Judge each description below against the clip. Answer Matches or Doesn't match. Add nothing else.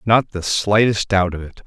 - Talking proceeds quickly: Matches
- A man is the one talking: Matches